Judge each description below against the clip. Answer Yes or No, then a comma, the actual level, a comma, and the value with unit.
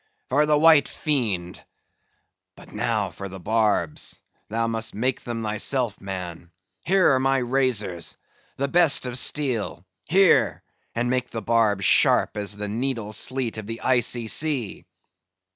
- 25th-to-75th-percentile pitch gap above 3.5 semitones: Yes, average, 4.3 semitones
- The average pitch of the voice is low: Yes, low, 115 Hz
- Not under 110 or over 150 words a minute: Yes, average, 140 wpm